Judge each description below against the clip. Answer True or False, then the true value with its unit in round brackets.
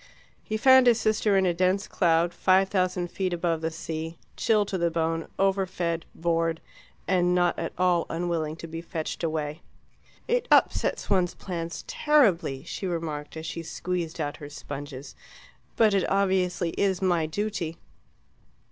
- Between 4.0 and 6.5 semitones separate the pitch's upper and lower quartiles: False (2.7 semitones)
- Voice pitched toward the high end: False (175 Hz)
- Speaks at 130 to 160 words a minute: True (155 wpm)